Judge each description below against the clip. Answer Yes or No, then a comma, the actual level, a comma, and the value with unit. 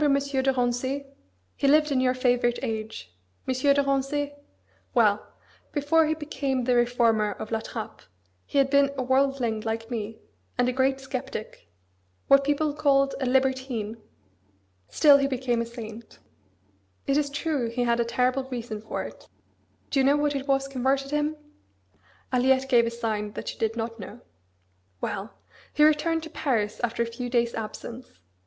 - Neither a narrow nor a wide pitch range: Yes, average, 3.0 semitones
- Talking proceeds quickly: No, average, 165 wpm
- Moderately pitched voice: No, very high, 260 Hz